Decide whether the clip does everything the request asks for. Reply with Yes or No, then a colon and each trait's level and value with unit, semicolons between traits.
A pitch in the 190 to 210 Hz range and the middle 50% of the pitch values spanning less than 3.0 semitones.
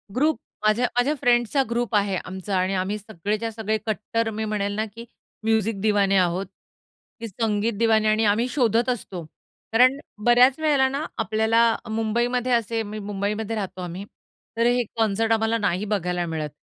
No: high, 220 Hz; narrow, 2.5 semitones